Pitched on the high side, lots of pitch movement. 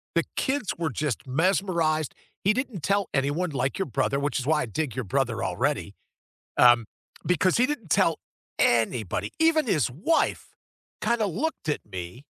No: medium, 155 Hz; wide, 7.4 semitones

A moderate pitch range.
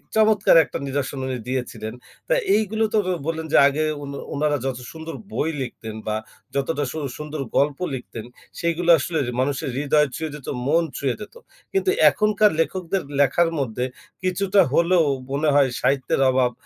Yes: average, 4.2 semitones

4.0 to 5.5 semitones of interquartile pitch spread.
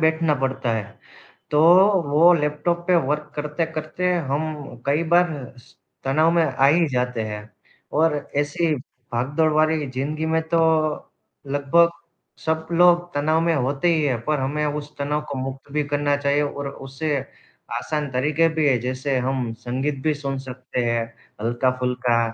No: average, 3.0 semitones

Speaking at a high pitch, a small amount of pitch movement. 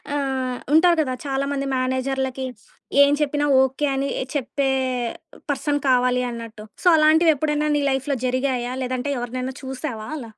Yes: very high, 265 Hz; narrow, 2.3 semitones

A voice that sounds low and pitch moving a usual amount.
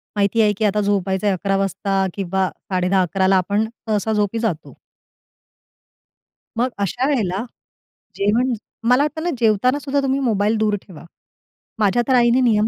No: high, 210 Hz; average, 3.6 semitones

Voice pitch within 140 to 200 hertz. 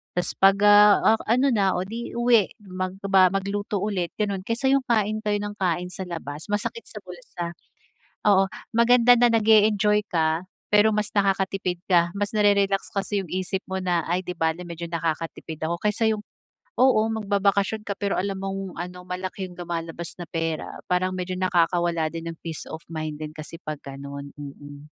Yes: high, 190 Hz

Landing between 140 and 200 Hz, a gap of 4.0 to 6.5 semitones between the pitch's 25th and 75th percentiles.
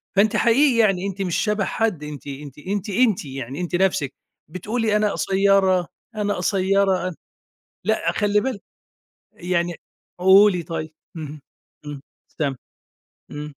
Yes: high, 190 Hz; average, 4.4 semitones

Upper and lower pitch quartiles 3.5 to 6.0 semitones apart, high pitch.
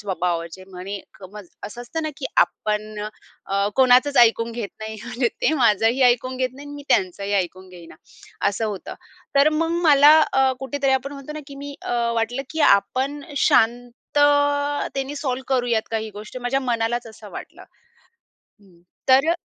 Yes: average, 4.7 semitones; high, 245 Hz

